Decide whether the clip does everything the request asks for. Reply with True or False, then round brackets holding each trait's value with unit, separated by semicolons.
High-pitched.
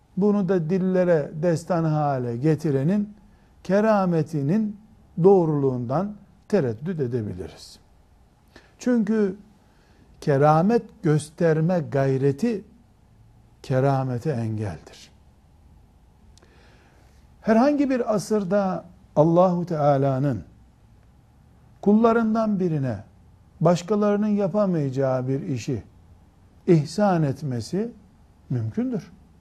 False (160 Hz)